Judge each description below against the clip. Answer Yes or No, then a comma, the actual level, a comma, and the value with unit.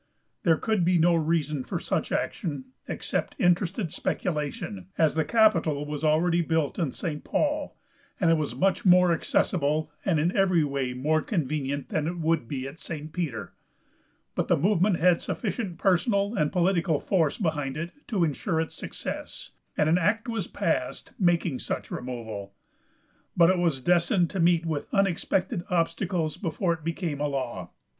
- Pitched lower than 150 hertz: No, medium, 165 Hz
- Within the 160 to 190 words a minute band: Yes, average, 165 wpm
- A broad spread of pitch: No, average, 3.3 semitones